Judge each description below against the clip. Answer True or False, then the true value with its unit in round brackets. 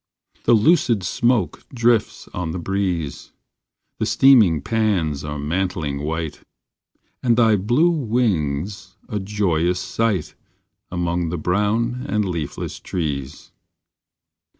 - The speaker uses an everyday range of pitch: False (5.7 semitones)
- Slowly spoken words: True (110 wpm)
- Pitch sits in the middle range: False (95 Hz)